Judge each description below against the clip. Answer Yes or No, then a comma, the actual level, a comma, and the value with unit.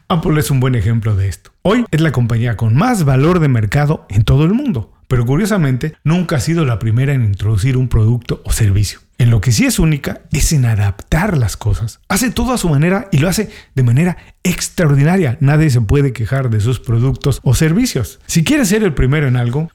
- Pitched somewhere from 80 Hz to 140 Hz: Yes, low, 135 Hz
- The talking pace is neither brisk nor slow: No, fast, 215 wpm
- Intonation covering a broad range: Yes, wide, 5.9 semitones